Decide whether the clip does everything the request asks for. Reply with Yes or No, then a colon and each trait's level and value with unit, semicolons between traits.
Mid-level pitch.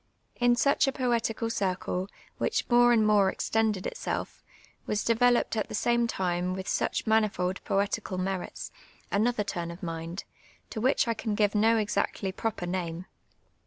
No: high, 210 Hz